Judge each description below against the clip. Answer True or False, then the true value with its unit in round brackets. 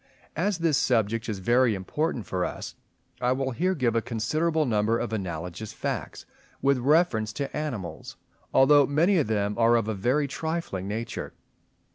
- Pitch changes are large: True (5.7 semitones)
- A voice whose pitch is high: False (120 Hz)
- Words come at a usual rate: True (160 wpm)